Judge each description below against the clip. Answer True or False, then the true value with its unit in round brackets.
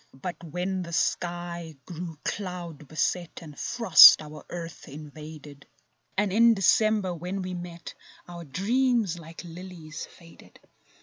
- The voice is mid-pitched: True (175 Hz)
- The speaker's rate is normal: False (125 wpm)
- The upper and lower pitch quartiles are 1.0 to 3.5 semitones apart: True (2.9 semitones)